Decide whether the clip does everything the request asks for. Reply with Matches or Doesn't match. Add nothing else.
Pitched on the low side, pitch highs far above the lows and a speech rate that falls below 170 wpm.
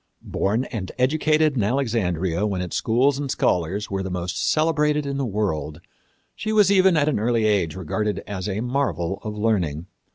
Doesn't match